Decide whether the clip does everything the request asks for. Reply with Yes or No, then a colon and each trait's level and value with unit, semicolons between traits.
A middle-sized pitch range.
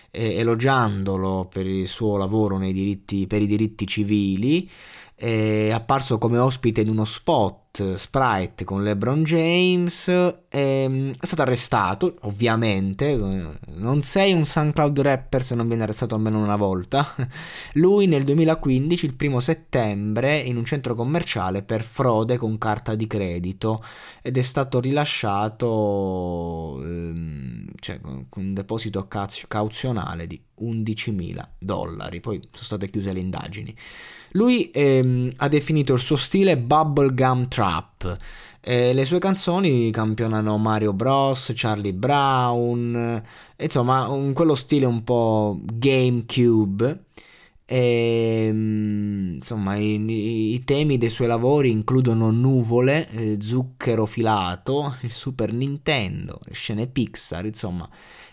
Yes: average, 4.4 semitones